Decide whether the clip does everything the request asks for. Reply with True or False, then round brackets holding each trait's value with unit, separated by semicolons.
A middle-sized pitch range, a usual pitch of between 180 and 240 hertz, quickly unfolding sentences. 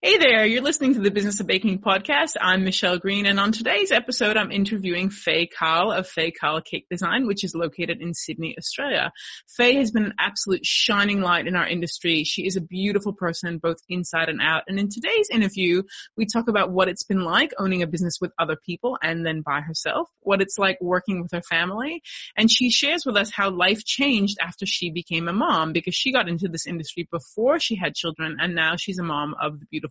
True (3.9 semitones; 190 Hz; 220 wpm)